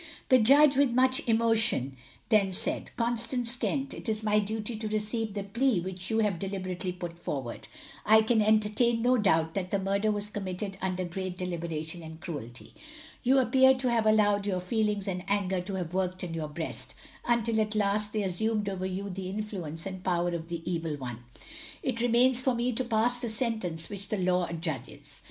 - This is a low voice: No, high, 200 Hz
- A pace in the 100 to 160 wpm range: No, average, 190 wpm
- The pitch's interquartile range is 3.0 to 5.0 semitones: Yes, average, 3.9 semitones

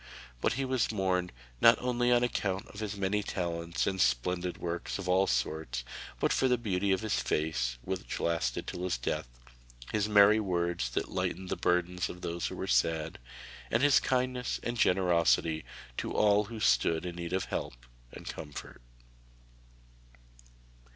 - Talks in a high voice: No, very low, 90 Hz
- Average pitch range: Yes, average, 4.1 semitones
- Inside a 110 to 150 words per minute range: No, average, 165 wpm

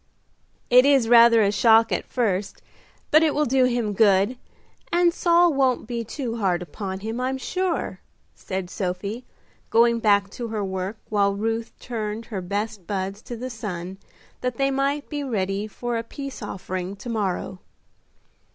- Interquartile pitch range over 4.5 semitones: No, average, 4.1 semitones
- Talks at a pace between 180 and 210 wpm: No, average, 160 wpm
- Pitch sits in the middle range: No, high, 225 Hz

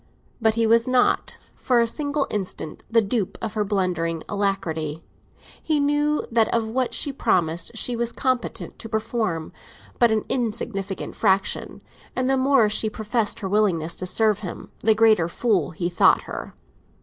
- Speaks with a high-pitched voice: Yes, high, 220 Hz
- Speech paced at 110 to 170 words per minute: Yes, average, 160 wpm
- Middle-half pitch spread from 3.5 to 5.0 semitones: Yes, average, 3.8 semitones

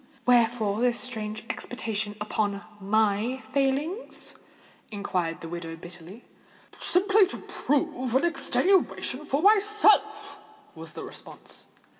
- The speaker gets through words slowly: Yes, slow, 105 wpm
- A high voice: Yes, high, 245 Hz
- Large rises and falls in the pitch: Yes, wide, 8.3 semitones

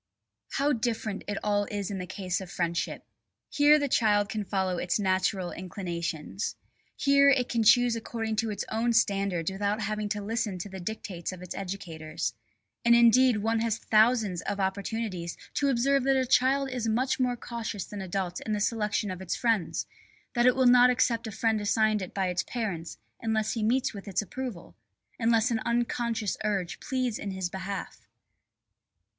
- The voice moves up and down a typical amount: Yes, average, 3.7 semitones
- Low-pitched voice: No, high, 215 Hz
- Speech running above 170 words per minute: Yes, average, 180 wpm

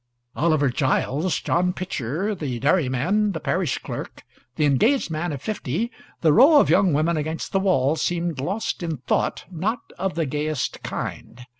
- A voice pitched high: No, medium, 165 Hz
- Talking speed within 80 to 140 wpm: No, average, 160 wpm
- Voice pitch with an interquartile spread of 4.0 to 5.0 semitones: Yes, average, 4.7 semitones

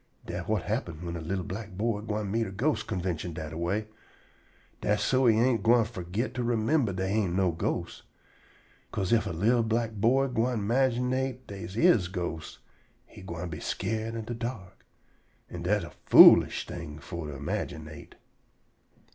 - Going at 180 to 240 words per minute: No, average, 170 wpm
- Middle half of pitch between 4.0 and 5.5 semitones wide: Yes, average, 4.8 semitones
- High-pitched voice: No, low, 105 Hz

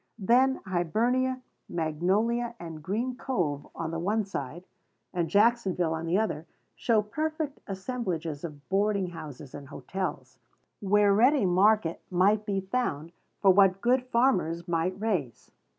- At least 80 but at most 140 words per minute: Yes, slow, 135 wpm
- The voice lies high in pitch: Yes, high, 195 Hz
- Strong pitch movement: Yes, wide, 5.8 semitones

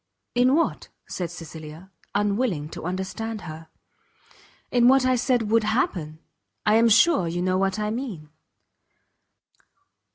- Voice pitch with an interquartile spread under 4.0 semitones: No, wide, 5.5 semitones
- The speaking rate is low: Yes, slow, 130 wpm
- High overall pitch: Yes, high, 205 Hz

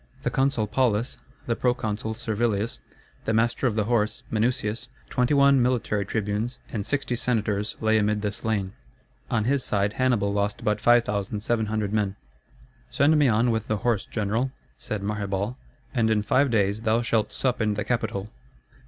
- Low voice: Yes, low, 110 Hz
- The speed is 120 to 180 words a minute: Yes, average, 155 wpm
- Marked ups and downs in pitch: No, narrow, 2.6 semitones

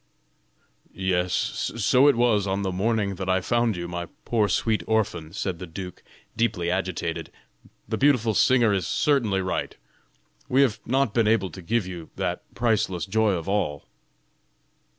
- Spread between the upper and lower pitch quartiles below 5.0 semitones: Yes, average, 3.9 semitones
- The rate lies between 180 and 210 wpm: No, average, 155 wpm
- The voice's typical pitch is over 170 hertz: No, low, 100 Hz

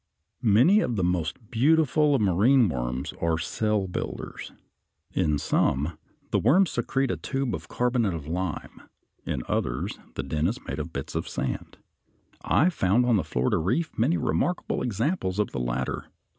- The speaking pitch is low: Yes, low, 100 Hz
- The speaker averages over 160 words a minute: Yes, average, 170 wpm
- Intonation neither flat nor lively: No, wide, 8.7 semitones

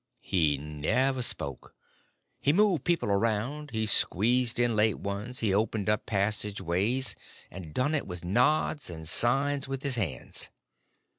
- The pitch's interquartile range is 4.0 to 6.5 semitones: Yes, average, 5.3 semitones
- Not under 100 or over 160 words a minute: Yes, average, 140 wpm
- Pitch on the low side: Yes, low, 110 Hz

